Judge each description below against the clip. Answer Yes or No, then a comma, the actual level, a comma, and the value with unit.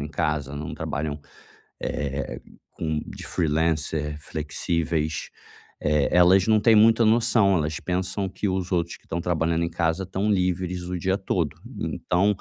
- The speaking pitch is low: Yes, very low, 85 Hz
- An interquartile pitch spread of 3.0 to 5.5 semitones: Yes, average, 3.6 semitones